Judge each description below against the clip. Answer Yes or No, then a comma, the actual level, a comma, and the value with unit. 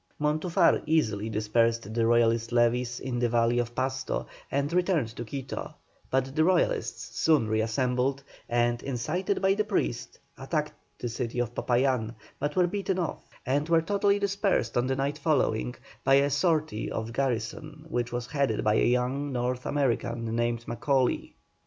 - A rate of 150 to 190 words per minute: Yes, average, 165 wpm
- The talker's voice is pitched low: Yes, low, 130 Hz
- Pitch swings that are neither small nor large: Yes, average, 4.3 semitones